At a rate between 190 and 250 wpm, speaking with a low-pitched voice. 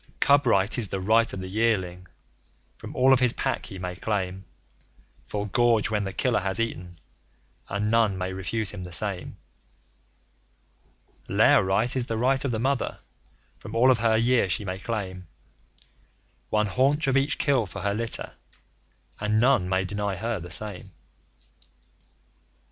No: average, 160 wpm; low, 105 Hz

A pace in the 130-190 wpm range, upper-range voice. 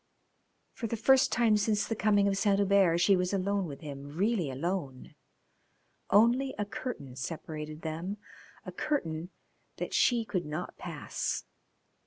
Yes: average, 145 wpm; high, 195 Hz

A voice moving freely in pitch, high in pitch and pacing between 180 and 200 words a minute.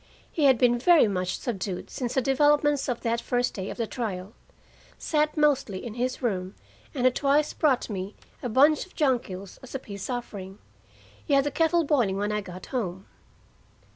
Yes: wide, 5.8 semitones; high, 245 Hz; average, 190 wpm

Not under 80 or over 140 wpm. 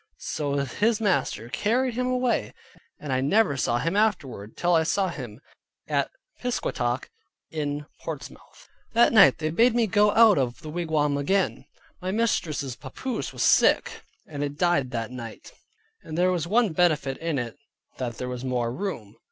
No: average, 165 wpm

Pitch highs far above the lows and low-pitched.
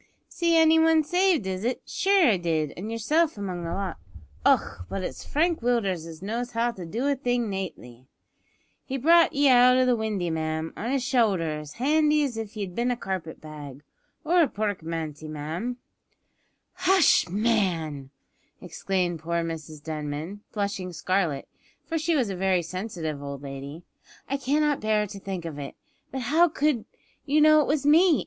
No: wide, 8.8 semitones; high, 205 Hz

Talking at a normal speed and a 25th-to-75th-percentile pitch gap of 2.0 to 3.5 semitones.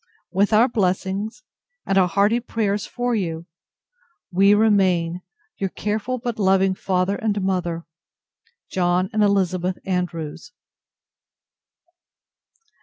No: slow, 105 wpm; average, 2.7 semitones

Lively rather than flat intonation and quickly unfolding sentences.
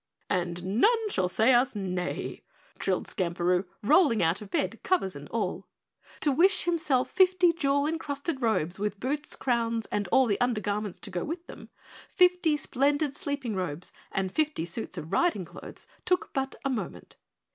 No: wide, 8.1 semitones; average, 160 wpm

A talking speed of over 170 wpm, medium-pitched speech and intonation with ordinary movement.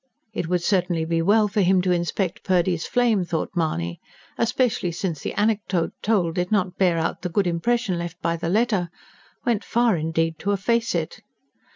Yes: average, 180 wpm; medium, 180 Hz; average, 3.8 semitones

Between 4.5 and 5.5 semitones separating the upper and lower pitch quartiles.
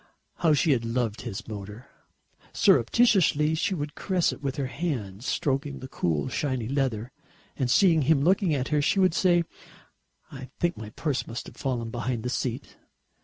Yes: average, 5.2 semitones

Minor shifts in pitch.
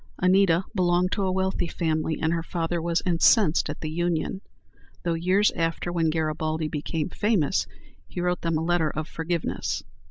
Yes: narrow, 2.0 semitones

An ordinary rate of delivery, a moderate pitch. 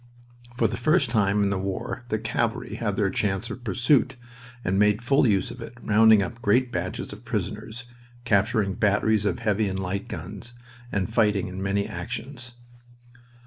No: average, 170 wpm; low, 105 Hz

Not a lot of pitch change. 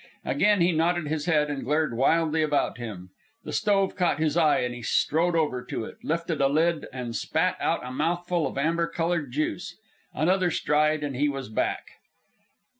No: average, 3.4 semitones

